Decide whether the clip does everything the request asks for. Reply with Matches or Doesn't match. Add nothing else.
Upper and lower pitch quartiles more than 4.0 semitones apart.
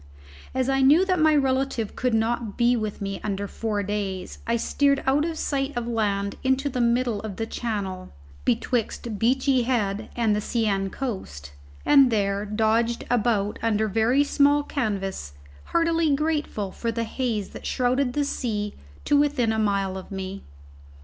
Matches